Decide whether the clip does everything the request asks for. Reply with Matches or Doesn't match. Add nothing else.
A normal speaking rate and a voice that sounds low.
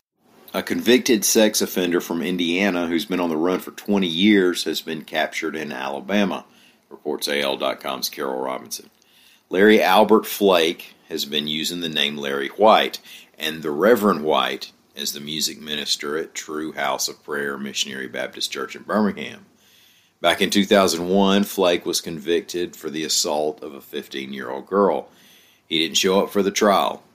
Matches